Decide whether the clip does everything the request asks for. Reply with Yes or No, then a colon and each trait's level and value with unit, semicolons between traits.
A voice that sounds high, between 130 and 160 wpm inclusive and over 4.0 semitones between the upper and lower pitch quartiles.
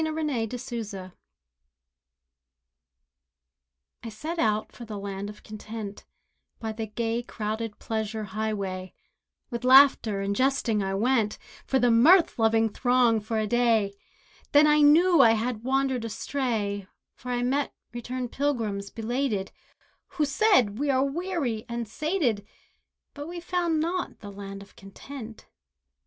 Yes: high, 230 Hz; average, 140 wpm; average, 4.4 semitones